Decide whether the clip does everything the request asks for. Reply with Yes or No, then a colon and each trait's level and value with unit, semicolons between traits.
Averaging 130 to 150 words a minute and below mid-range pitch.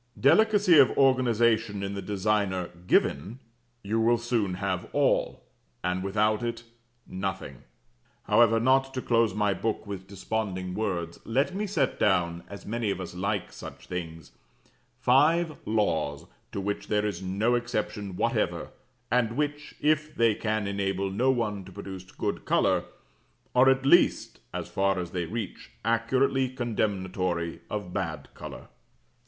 Yes: average, 145 wpm; low, 105 Hz